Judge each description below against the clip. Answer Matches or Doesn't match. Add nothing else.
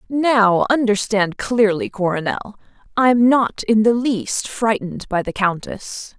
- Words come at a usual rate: Doesn't match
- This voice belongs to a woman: Matches